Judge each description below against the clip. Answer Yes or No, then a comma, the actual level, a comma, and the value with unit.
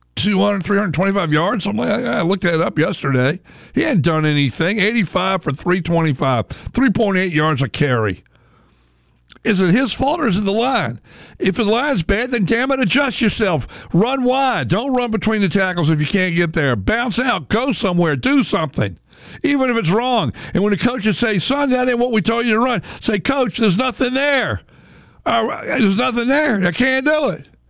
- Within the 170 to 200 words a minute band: Yes, average, 185 wpm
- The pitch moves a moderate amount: No, wide, 6.5 semitones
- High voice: Yes, high, 205 Hz